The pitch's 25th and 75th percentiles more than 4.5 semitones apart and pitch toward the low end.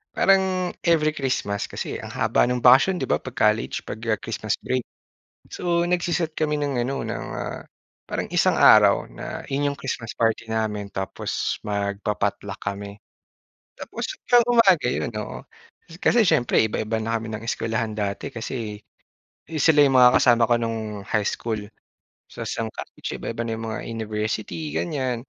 Yes: average, 5.0 semitones; low, 115 Hz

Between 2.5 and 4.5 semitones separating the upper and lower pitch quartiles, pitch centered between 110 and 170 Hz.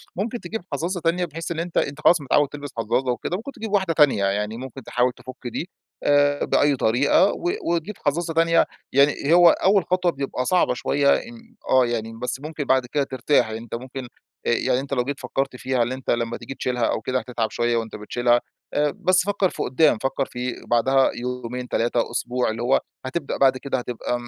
No: average, 5.2 semitones; low, 135 Hz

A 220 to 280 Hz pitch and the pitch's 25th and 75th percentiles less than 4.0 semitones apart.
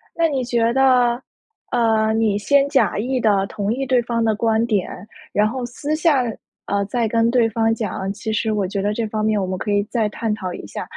Yes: high, 225 Hz; average, 2.7 semitones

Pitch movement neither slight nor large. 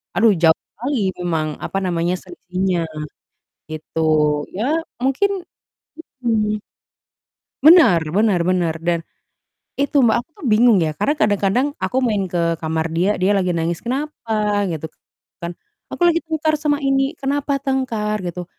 No: wide, 7.7 semitones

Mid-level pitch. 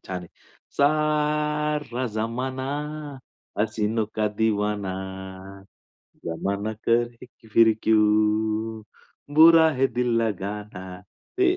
No: low, 115 Hz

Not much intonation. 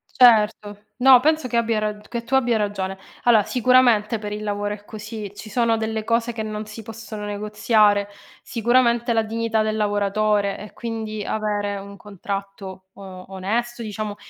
Yes: narrow, 2.0 semitones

